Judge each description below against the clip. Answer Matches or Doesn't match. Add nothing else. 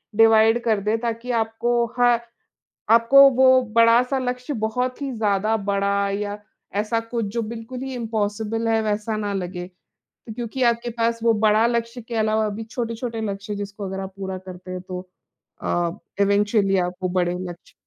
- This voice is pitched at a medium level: Doesn't match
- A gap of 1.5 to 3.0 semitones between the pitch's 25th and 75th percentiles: Matches